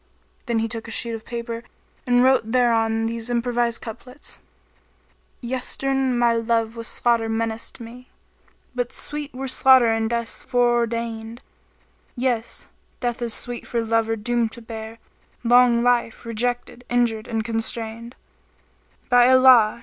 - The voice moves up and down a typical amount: No, narrow, 1.5 semitones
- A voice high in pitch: Yes, high, 235 Hz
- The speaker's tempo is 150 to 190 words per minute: No, average, 140 wpm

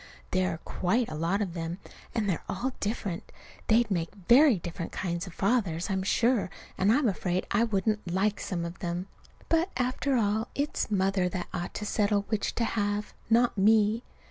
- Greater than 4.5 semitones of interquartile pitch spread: No, average, 4.0 semitones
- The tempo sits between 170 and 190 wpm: Yes, average, 180 wpm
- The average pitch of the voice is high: Yes, high, 205 Hz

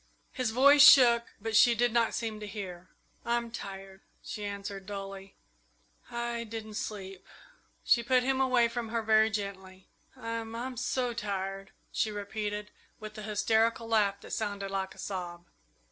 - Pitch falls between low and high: No, high, 215 Hz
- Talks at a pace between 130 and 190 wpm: Yes, average, 160 wpm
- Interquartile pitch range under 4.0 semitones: Yes, average, 3.0 semitones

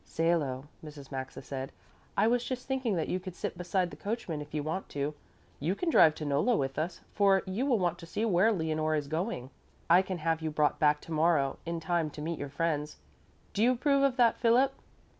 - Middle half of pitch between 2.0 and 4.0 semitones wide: No, average, 5.3 semitones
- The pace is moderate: No, fast, 220 wpm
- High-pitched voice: No, medium, 165 Hz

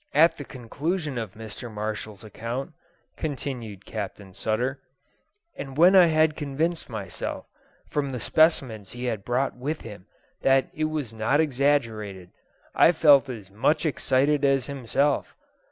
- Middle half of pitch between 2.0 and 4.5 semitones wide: No, average, 5.1 semitones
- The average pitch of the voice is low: Yes, low, 130 Hz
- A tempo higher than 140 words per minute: No, slow, 135 wpm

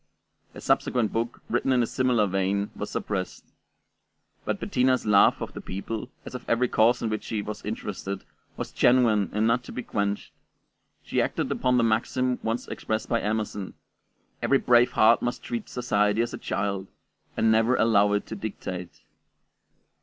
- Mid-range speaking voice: No, low, 110 Hz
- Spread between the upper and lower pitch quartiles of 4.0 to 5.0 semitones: No, average, 2.9 semitones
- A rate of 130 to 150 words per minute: No, average, 170 wpm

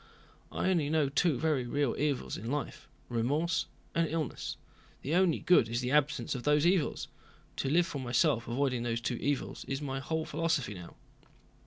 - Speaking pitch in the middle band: Yes, medium, 145 Hz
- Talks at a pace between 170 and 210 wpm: Yes, average, 175 wpm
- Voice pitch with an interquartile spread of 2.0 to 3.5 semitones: No, average, 4.3 semitones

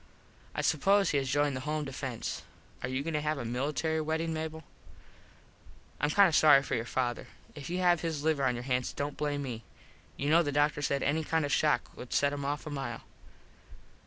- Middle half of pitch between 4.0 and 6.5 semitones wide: No, average, 2.7 semitones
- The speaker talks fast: Yes, fast, 220 wpm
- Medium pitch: Yes, medium, 145 Hz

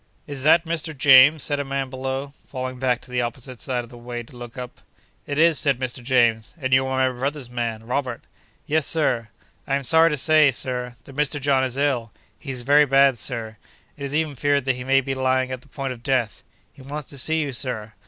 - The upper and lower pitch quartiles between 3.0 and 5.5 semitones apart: No, narrow, 2.4 semitones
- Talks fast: Yes, fast, 230 wpm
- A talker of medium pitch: No, low, 130 Hz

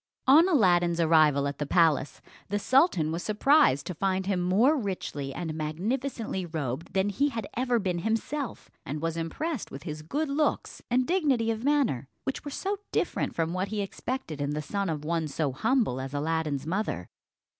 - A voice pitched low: No, medium, 185 Hz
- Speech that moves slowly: No, average, 180 wpm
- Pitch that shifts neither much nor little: No, wide, 8.3 semitones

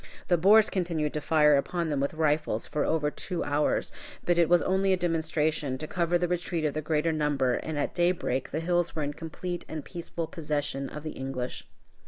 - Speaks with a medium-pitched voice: Yes, medium, 160 Hz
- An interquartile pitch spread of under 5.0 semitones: Yes, average, 2.8 semitones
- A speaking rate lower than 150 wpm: No, fast, 205 wpm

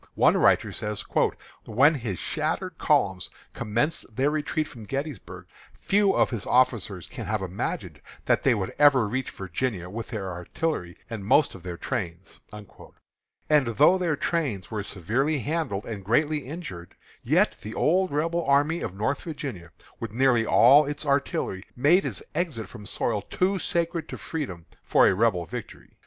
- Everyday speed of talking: Yes, average, 160 wpm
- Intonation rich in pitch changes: Yes, wide, 7.1 semitones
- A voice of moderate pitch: No, low, 125 Hz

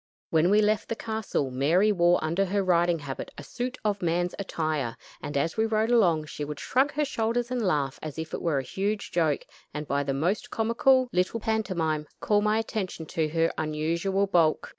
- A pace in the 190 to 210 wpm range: Yes, average, 200 wpm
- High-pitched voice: No, medium, 175 Hz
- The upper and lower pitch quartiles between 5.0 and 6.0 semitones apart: Yes, wide, 5.6 semitones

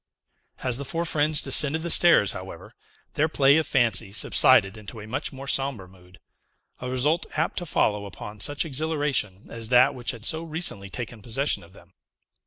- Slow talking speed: No, average, 180 wpm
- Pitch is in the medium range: No, low, 125 Hz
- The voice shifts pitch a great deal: Yes, wide, 6.3 semitones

